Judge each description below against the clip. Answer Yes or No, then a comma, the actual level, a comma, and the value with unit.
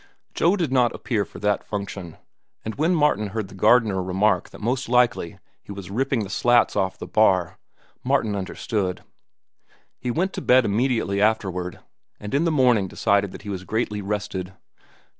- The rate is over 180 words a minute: No, average, 170 wpm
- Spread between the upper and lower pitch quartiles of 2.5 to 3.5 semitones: No, average, 4.2 semitones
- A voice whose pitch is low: Yes, low, 105 Hz